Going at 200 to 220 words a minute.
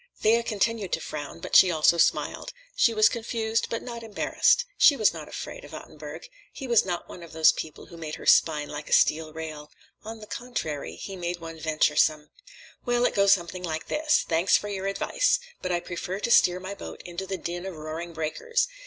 Yes: fast, 205 wpm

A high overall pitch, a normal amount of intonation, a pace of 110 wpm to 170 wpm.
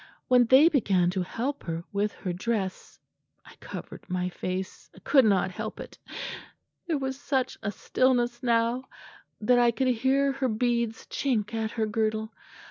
Yes: high, 230 Hz; average, 4.1 semitones; average, 160 wpm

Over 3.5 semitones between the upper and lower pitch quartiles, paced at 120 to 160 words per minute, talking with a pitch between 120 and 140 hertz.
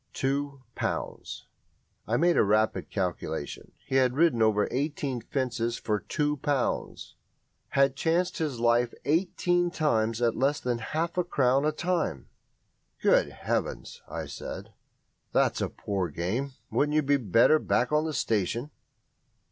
Yes: average, 4.8 semitones; average, 140 wpm; low, 135 Hz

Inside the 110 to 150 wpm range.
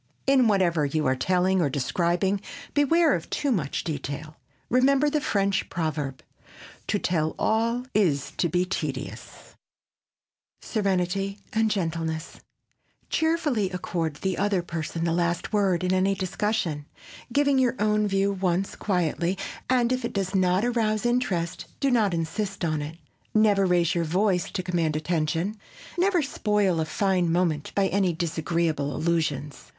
Yes: average, 145 wpm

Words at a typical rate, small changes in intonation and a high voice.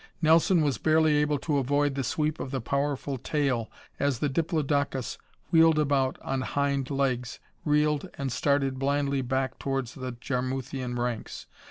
No: average, 150 wpm; narrow, 2.2 semitones; medium, 140 Hz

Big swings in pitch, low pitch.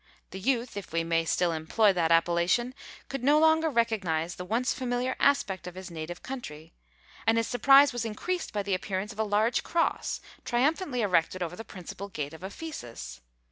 No: wide, 6.5 semitones; high, 205 Hz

